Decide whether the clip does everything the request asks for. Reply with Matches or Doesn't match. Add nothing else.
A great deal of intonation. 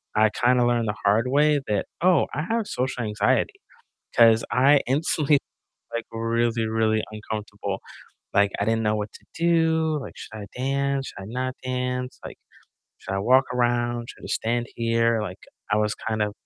Doesn't match